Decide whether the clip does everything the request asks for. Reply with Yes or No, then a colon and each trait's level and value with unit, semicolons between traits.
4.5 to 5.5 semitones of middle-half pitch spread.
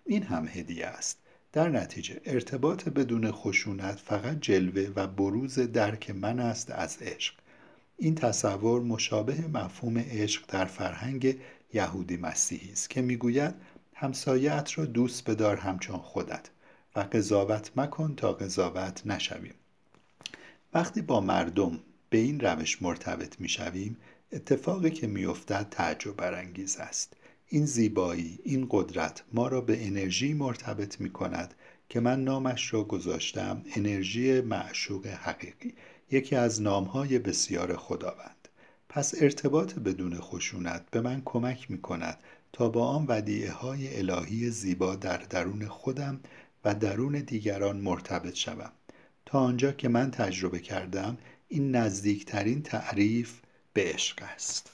Yes: average, 5.0 semitones